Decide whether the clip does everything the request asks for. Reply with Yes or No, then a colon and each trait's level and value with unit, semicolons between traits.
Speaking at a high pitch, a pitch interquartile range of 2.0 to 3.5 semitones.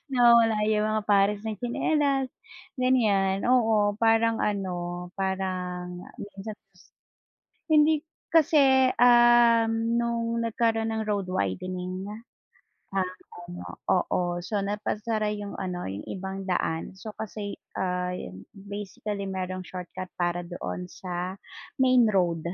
No: high, 205 Hz; average, 3.9 semitones